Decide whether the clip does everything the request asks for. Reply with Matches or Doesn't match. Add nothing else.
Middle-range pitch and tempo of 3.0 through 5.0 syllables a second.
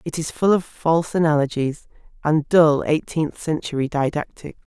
Matches